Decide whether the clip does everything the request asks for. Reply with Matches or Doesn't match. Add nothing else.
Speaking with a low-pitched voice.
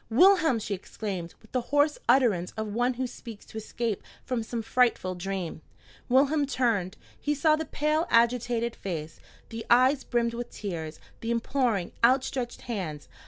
Doesn't match